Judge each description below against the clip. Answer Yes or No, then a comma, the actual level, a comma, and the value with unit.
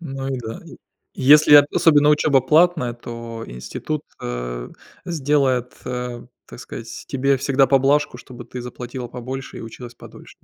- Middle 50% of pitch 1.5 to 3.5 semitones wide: Yes, average, 3.2 semitones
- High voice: No, low, 130 Hz